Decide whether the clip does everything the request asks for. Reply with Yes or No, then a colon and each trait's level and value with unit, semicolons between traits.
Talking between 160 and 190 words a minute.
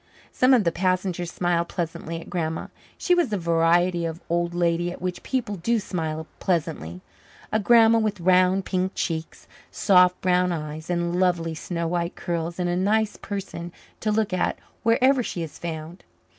Yes: average, 170 wpm